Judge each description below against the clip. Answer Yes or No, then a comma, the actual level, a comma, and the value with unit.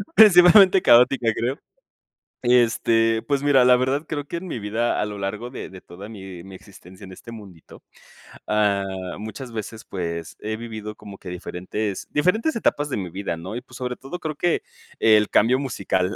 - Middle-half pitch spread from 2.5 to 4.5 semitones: No, average, 5.2 semitones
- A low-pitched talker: Yes, low, 115 Hz